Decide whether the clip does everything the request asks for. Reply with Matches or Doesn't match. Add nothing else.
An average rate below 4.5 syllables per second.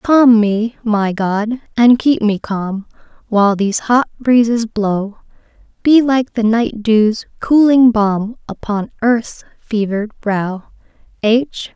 Matches